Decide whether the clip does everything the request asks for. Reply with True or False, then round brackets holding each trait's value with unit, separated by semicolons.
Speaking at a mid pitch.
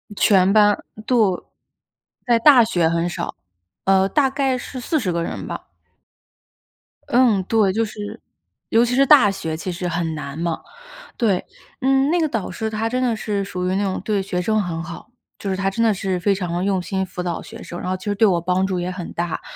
False (195 Hz)